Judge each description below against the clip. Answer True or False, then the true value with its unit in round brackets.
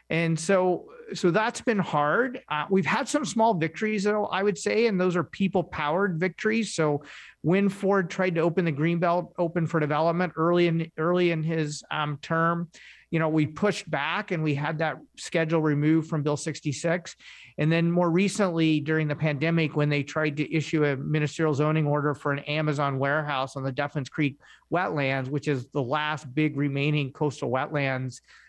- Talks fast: False (180 wpm)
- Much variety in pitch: False (3.5 semitones)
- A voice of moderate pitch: True (160 Hz)